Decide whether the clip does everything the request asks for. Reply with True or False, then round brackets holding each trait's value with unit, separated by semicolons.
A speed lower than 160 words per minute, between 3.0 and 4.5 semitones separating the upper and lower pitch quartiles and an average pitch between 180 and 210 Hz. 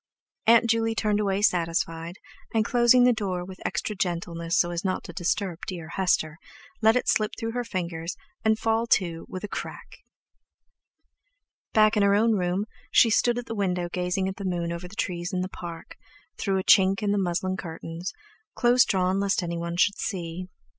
False (185 wpm; 3.6 semitones; 190 Hz)